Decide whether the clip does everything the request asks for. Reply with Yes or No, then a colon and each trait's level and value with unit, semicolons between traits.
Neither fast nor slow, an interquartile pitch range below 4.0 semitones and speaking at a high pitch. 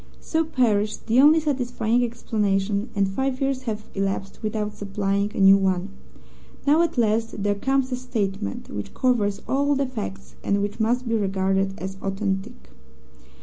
No: average, 155 wpm; average, 4.4 semitones; high, 215 Hz